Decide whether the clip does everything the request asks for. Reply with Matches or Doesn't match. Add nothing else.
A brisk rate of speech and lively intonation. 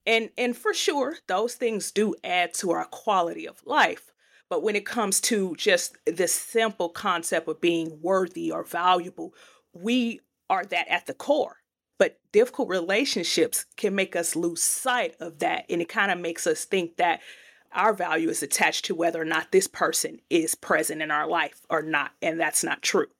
Doesn't match